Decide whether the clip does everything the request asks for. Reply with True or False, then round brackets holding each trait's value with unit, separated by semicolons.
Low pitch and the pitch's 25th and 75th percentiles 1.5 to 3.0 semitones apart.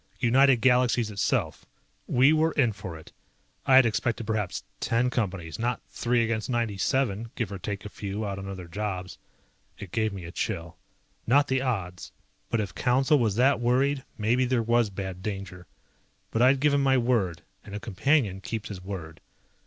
False (115 Hz; 4.5 semitones)